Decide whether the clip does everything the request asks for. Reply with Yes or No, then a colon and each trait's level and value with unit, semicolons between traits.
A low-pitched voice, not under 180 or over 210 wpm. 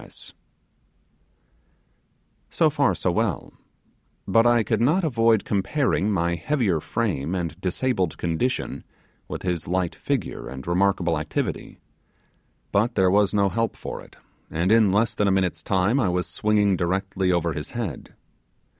No: very low, 95 Hz; average, 140 wpm